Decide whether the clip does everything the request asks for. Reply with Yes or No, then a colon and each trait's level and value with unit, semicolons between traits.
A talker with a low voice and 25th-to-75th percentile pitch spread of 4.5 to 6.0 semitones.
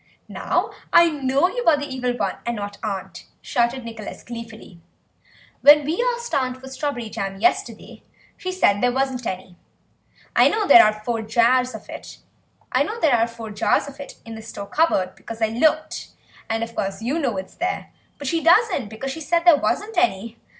No: high, 245 Hz; wide, 5.5 semitones